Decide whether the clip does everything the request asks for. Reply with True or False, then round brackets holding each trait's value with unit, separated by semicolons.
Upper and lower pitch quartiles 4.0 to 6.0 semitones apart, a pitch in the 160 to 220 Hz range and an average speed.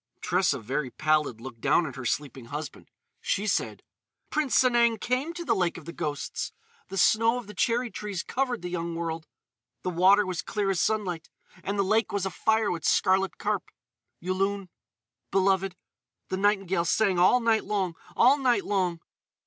True (4.4 semitones; 190 Hz; 160 wpm)